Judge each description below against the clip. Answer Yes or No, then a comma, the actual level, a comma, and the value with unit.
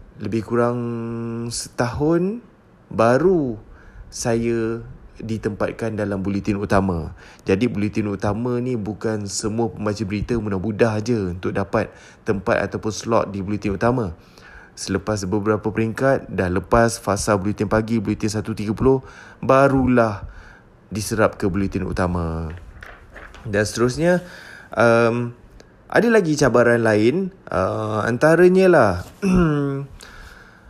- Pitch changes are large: No, average, 2.8 semitones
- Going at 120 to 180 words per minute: No, average, 100 wpm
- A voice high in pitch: No, low, 110 Hz